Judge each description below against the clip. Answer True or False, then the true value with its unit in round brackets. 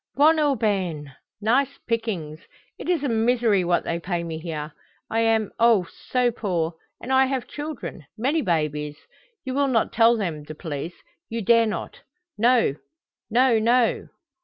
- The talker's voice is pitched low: False (225 Hz)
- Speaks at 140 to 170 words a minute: True (155 wpm)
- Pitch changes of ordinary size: False (6.7 semitones)